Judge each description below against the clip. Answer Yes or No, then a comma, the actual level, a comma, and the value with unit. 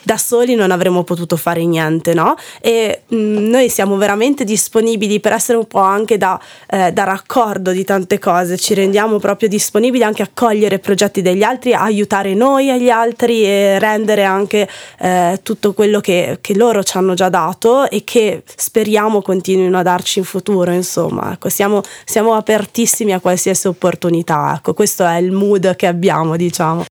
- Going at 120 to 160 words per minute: No, fast, 170 wpm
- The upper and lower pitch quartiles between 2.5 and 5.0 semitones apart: Yes, average, 3.0 semitones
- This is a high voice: Yes, high, 200 Hz